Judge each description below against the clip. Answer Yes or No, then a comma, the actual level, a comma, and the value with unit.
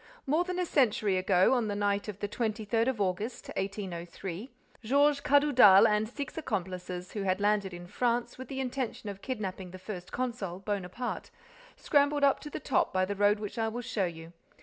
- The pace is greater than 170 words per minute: Yes, average, 195 wpm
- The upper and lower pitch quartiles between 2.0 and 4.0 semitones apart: No, average, 5.0 semitones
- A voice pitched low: No, high, 210 Hz